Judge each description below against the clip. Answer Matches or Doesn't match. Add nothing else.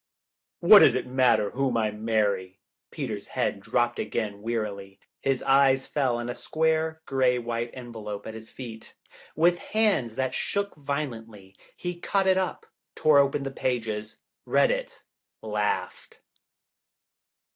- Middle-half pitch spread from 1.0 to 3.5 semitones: Doesn't match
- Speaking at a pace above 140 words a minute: Doesn't match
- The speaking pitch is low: Matches